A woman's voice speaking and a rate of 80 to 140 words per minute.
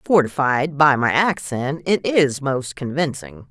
Yes: female; slow, 135 wpm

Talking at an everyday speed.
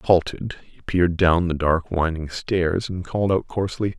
Yes: average, 180 wpm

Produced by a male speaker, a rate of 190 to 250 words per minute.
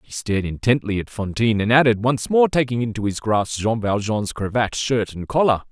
Yes: male; average, 200 wpm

